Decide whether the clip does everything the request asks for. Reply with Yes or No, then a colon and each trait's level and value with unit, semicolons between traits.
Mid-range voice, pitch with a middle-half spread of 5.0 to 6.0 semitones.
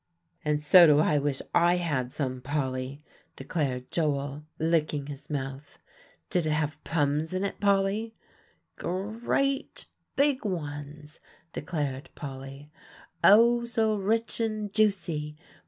Yes: medium, 155 Hz; wide, 5.6 semitones